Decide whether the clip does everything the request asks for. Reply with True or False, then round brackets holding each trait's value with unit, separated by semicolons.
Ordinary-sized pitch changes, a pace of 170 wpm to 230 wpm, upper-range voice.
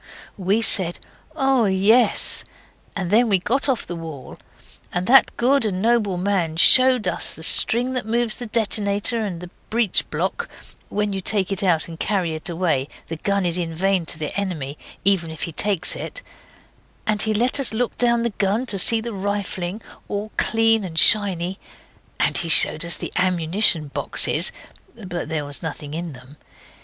True (4.7 semitones; 180 wpm; 195 Hz)